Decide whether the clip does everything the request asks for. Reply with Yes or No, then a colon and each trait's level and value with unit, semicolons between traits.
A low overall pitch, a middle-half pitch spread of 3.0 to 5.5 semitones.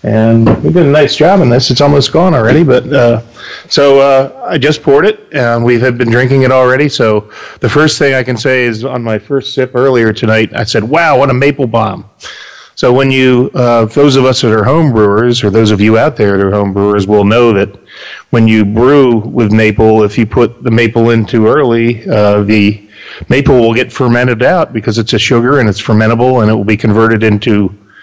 Yes: low, 120 Hz; average, 3.3 semitones